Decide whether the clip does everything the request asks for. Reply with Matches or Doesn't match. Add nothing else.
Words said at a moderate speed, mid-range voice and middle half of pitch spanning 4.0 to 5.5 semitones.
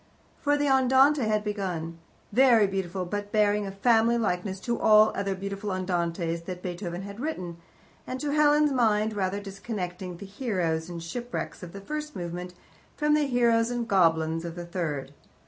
Doesn't match